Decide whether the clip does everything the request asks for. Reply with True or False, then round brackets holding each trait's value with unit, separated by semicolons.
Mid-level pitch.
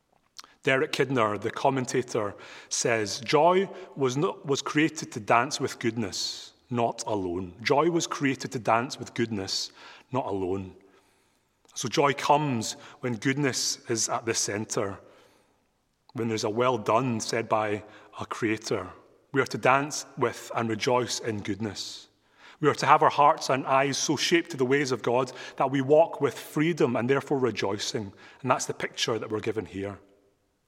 False (125 Hz)